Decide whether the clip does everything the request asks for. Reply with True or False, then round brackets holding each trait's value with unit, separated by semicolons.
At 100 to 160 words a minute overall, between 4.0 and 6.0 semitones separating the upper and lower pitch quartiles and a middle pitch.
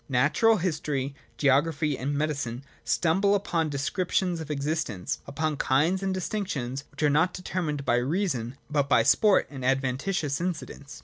True (140 wpm; 4.6 semitones; 150 Hz)